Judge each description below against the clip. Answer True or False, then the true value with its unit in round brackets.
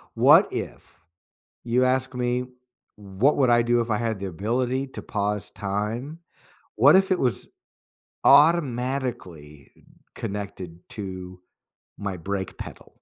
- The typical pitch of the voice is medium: False (115 Hz)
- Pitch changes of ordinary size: True (4.7 semitones)